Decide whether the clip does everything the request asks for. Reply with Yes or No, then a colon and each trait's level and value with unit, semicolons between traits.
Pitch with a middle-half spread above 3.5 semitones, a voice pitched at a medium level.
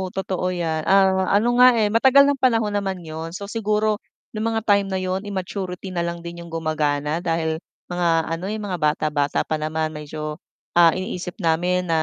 Yes: average, 4.0 semitones; medium, 180 Hz